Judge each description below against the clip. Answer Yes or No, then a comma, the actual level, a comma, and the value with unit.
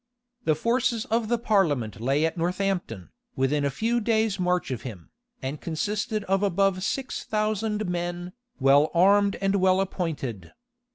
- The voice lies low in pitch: No, medium, 185 Hz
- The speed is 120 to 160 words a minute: Yes, average, 150 wpm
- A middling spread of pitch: No, wide, 6.0 semitones